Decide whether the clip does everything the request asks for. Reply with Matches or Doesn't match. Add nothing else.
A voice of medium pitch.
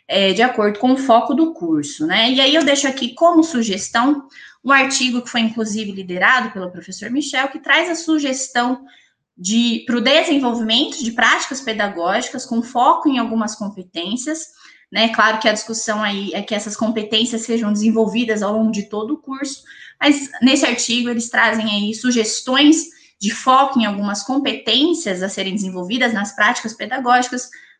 Doesn't match